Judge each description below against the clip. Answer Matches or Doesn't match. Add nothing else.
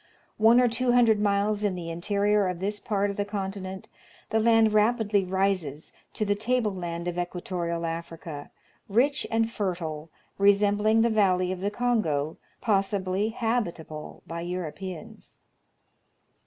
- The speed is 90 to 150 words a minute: Matches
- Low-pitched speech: Doesn't match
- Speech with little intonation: Doesn't match